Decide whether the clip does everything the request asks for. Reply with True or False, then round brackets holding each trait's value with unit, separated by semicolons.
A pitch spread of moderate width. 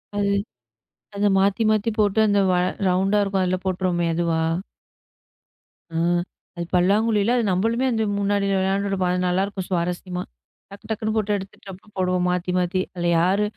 False (2.1 semitones)